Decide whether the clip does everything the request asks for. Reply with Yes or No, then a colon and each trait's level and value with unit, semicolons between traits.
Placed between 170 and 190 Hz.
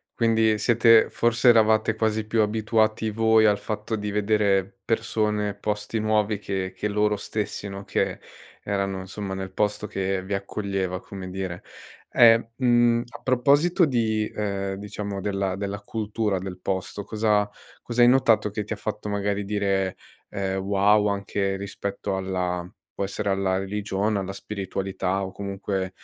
No: low, 105 Hz